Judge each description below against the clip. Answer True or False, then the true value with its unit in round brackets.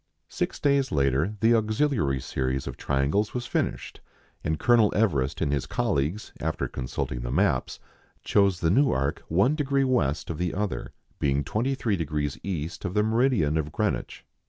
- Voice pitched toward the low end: True (90 Hz)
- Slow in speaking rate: False (155 wpm)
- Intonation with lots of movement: True (8.0 semitones)